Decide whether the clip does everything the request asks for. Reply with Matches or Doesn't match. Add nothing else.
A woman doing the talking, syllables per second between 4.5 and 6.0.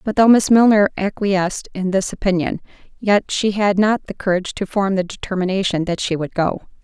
Matches